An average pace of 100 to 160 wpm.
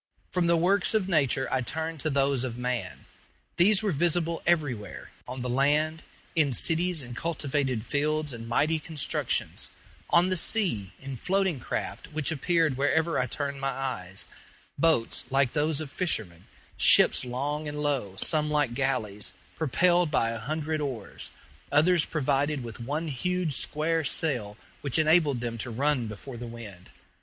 Yes: average, 155 wpm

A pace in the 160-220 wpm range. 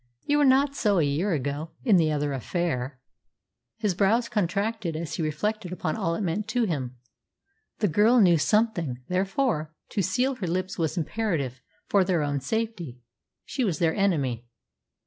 Yes: average, 165 wpm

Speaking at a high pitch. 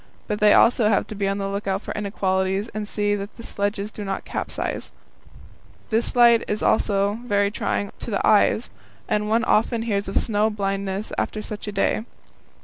Yes: high, 205 Hz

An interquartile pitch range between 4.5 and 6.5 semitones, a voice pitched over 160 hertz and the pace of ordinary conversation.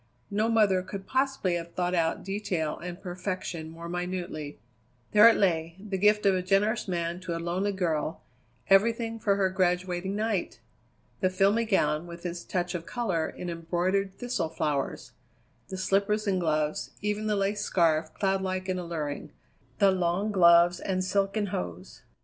No: average, 2.8 semitones; medium, 185 Hz; average, 160 wpm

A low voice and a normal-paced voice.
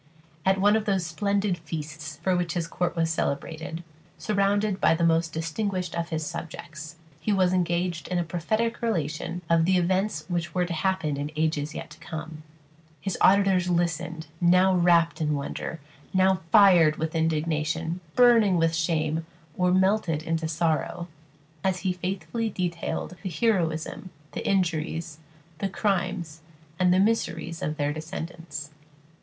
No: medium, 170 Hz; average, 150 wpm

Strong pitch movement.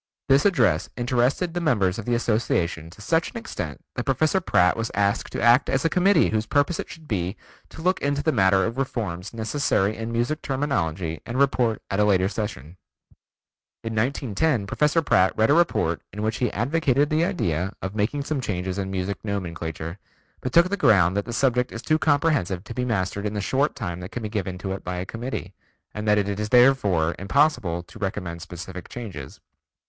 Yes: wide, 6.5 semitones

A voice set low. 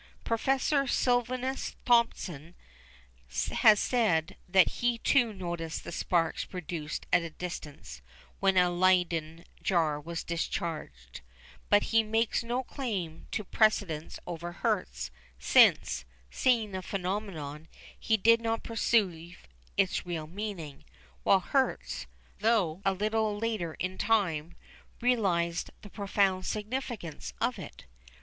No: medium, 185 Hz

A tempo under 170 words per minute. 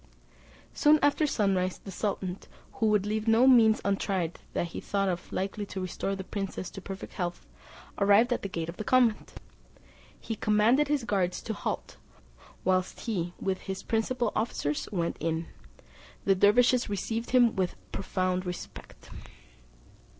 Yes: average, 150 wpm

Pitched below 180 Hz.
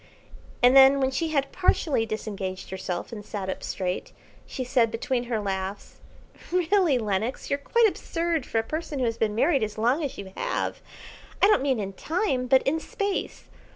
No: very high, 250 Hz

